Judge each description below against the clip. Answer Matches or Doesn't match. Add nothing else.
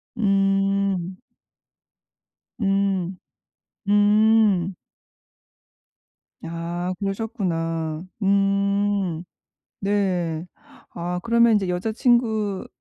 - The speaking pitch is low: Doesn't match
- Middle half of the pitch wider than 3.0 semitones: Doesn't match